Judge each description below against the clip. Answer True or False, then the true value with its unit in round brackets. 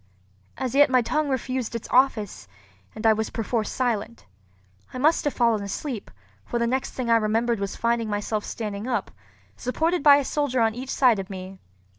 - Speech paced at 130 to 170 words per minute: False (185 wpm)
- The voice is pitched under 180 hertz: False (235 Hz)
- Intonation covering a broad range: False (3.3 semitones)